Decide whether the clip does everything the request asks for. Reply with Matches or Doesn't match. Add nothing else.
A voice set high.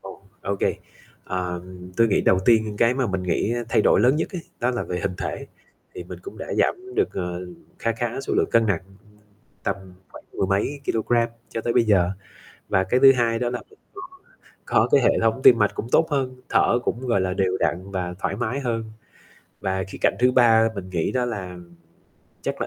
Doesn't match